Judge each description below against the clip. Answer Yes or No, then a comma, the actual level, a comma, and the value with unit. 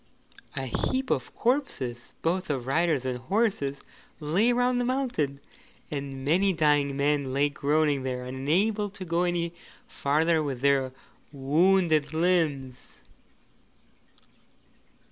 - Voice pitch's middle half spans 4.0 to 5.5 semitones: Yes, average, 5.1 semitones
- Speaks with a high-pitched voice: No, medium, 150 Hz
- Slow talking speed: Yes, slow, 115 wpm